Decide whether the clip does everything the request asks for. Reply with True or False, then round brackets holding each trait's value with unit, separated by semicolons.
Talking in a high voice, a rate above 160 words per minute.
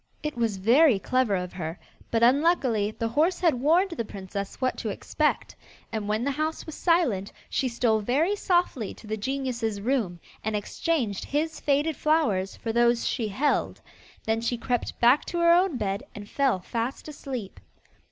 True (240 Hz; 170 wpm)